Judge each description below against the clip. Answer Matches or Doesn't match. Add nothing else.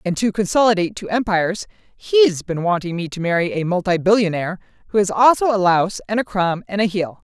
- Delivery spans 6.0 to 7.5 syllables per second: Matches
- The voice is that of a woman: Matches